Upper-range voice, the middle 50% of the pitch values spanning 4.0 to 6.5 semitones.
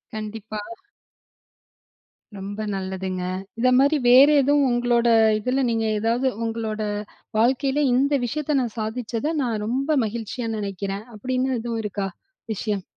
No: high, 230 Hz; average, 3.5 semitones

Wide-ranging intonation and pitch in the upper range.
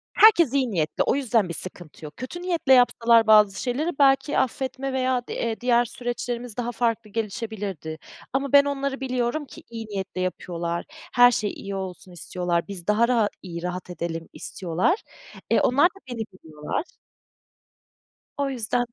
Yes: wide, 5.9 semitones; high, 230 Hz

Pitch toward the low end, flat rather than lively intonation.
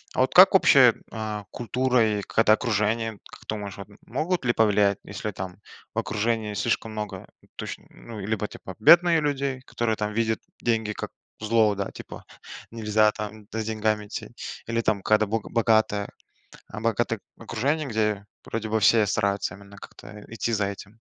Yes: low, 110 Hz; narrow, 1.7 semitones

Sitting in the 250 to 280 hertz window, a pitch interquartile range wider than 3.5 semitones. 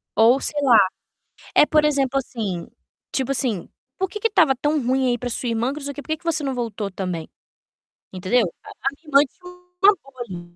Yes: very high, 265 Hz; average, 4.7 semitones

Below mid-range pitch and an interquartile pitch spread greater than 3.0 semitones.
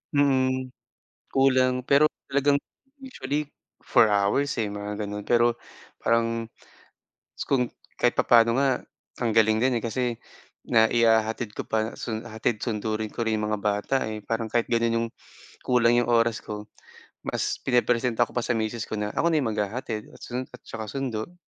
No: low, 115 Hz; average, 2.7 semitones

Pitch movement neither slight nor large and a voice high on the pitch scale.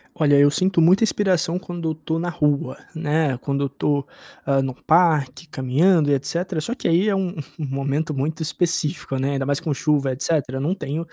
No: average, 3.5 semitones; medium, 155 Hz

